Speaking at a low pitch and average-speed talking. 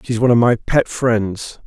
No: low, 115 Hz; fast, 215 wpm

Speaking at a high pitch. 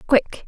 Yes: very high, 260 Hz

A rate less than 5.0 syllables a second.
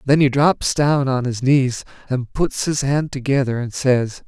Yes: 4.1 syllables/s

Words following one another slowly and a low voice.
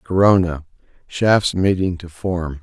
Yes: slow, 115 wpm; very low, 90 Hz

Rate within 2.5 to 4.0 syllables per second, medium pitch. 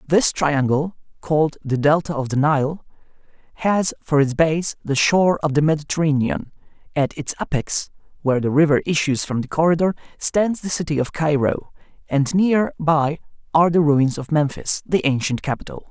No: 5.0 syllables/s; medium, 150 Hz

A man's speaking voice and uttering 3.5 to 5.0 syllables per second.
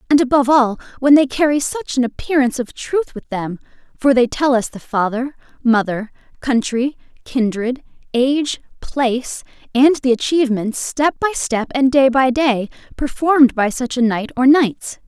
No: female; 4.8 syllables/s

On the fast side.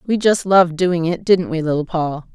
Yes: fast, 230 wpm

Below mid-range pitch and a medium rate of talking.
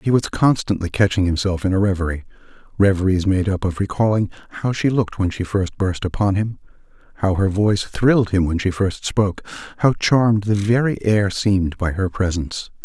Yes: low, 100 Hz; average, 180 wpm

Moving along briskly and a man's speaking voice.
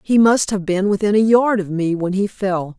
No: fast, 260 wpm; female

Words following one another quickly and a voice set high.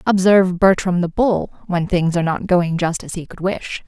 No: fast, 215 wpm; medium, 180 Hz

